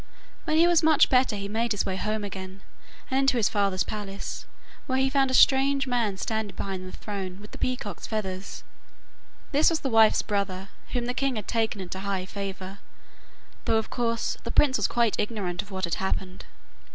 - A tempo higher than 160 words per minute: Yes, average, 190 wpm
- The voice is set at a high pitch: Yes, high, 215 Hz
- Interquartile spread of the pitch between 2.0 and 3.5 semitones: No, average, 4.6 semitones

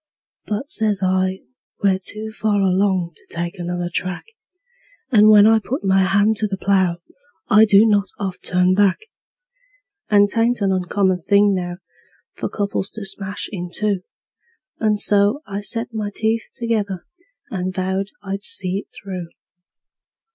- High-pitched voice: Yes, high, 200 Hz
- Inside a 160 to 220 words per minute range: No, average, 150 wpm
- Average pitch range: No, narrow, 2.1 semitones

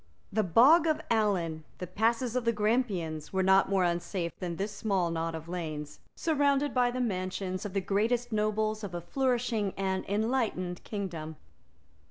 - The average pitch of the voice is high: Yes, high, 200 Hz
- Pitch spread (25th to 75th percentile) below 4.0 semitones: No, average, 4.6 semitones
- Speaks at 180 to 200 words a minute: No, average, 165 wpm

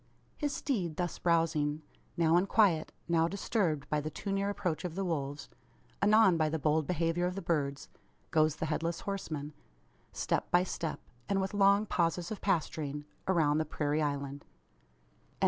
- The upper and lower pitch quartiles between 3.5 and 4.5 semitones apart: Yes, average, 3.9 semitones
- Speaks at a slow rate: No, average, 165 wpm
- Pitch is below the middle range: No, medium, 165 Hz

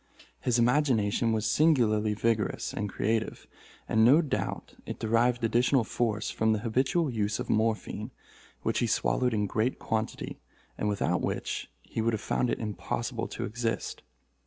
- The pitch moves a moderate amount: No, narrow, 2.2 semitones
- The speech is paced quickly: No, average, 155 wpm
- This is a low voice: Yes, low, 115 Hz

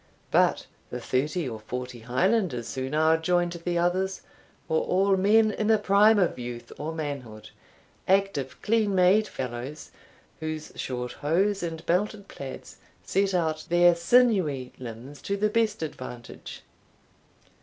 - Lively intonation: Yes, wide, 7.0 semitones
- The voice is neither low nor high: Yes, medium, 170 Hz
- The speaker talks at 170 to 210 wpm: No, slow, 135 wpm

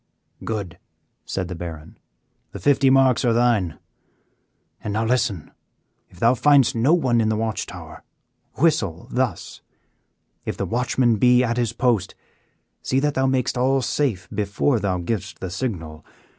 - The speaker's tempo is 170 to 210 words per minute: No, average, 150 wpm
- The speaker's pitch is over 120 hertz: No, low, 115 Hz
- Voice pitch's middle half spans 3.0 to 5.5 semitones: Yes, average, 4.8 semitones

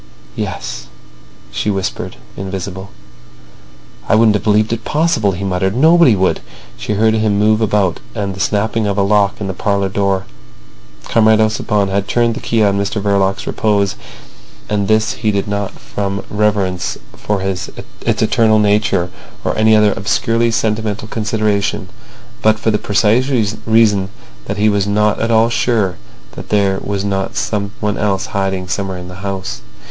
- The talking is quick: No, average, 160 wpm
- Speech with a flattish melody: Yes, narrow, 1.9 semitones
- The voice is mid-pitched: No, low, 105 Hz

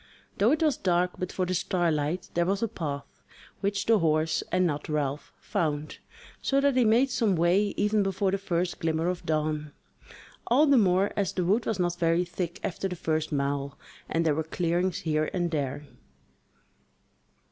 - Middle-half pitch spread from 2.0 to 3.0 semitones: No, average, 4.1 semitones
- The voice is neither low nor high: Yes, medium, 175 Hz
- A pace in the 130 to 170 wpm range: No, average, 180 wpm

